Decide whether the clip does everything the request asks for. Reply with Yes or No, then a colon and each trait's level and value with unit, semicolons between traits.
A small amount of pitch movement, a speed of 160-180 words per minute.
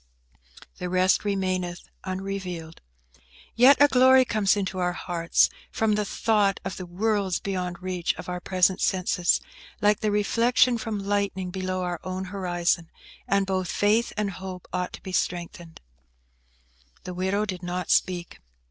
No: narrow, 2.2 semitones; average, 150 wpm